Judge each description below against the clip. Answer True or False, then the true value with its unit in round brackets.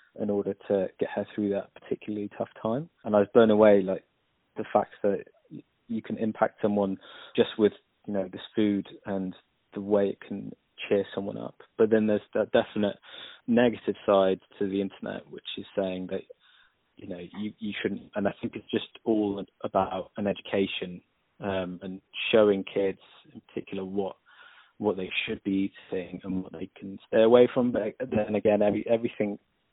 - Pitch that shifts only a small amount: True (2.1 semitones)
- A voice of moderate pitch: False (105 Hz)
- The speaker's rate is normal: True (180 wpm)